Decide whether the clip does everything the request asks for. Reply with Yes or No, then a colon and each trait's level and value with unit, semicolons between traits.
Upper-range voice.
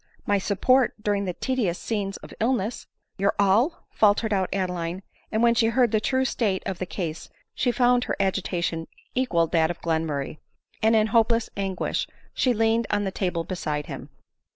Yes: high, 200 Hz